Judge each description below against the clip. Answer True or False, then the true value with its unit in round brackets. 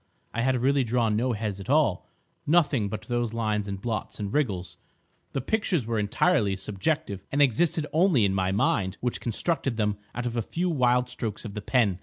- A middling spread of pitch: True (4.8 semitones)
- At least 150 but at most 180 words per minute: False (190 wpm)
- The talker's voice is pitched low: True (115 Hz)